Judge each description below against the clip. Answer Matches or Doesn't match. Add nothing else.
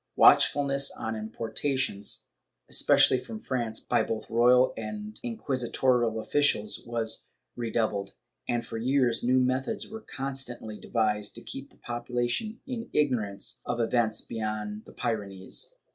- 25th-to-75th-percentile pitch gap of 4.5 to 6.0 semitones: Doesn't match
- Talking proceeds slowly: Matches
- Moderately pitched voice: Doesn't match